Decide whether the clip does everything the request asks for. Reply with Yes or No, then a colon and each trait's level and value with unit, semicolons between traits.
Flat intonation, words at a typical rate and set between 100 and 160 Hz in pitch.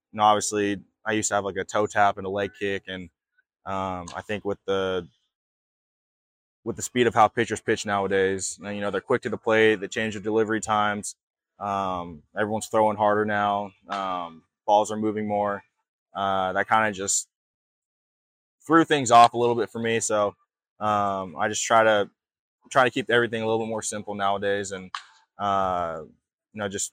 Yes: narrow, 1.9 semitones; average, 185 wpm; low, 105 Hz